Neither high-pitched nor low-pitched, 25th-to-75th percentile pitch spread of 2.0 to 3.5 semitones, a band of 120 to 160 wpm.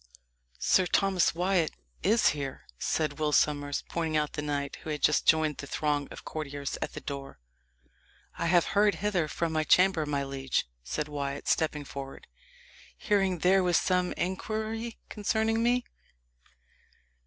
No: medium, 160 Hz; average, 4.8 semitones; average, 150 wpm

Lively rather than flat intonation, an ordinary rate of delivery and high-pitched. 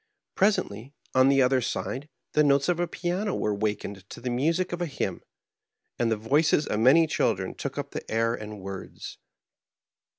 No: wide, 6.6 semitones; average, 175 wpm; low, 130 Hz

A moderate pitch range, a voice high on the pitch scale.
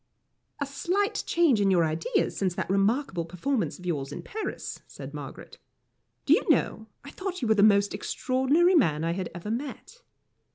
No: wide, 8.0 semitones; high, 215 Hz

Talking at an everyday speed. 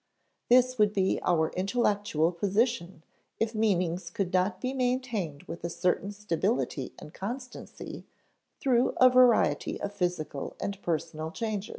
No: slow, 130 wpm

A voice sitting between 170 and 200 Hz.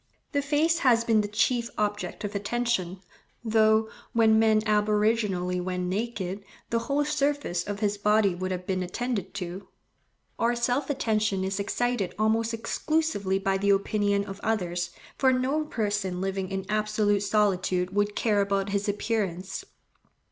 No: high, 210 Hz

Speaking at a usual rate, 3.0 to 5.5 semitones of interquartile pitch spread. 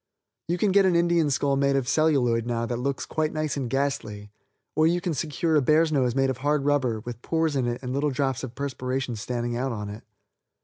No: fast, 225 wpm; average, 4.0 semitones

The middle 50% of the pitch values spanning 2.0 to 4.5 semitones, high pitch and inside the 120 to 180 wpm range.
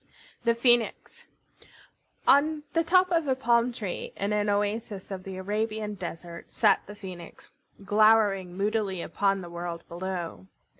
Yes: average, 3.7 semitones; high, 205 Hz; average, 140 wpm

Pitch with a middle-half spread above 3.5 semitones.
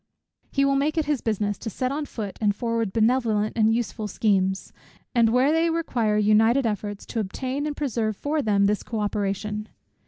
Yes: average, 4.1 semitones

